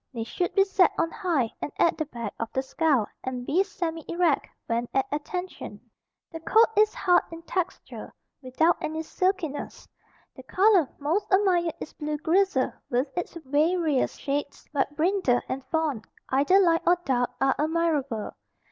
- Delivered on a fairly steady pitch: No, average, 4.9 semitones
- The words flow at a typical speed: Yes, average, 160 wpm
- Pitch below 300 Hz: No, very high, 320 Hz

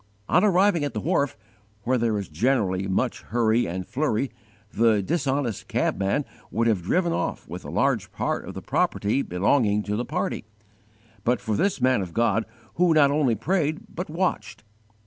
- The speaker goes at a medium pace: Yes, average, 170 wpm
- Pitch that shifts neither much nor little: No, wide, 6.0 semitones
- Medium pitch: No, low, 120 Hz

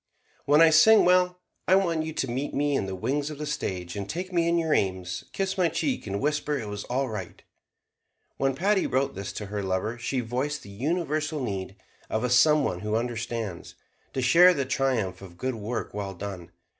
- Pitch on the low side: Yes, low, 130 Hz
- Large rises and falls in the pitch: Yes, wide, 7.3 semitones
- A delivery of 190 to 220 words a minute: Yes, fast, 205 wpm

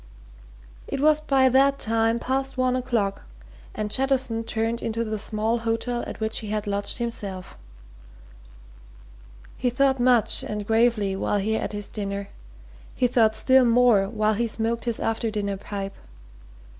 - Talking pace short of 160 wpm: Yes, average, 150 wpm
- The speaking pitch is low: No, high, 225 Hz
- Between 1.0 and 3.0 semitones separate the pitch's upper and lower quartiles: Yes, average, 2.7 semitones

